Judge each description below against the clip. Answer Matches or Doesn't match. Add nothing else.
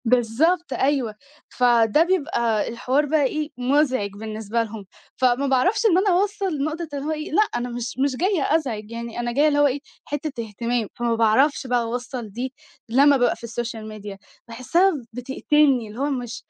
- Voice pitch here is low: Doesn't match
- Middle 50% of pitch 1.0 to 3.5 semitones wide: Doesn't match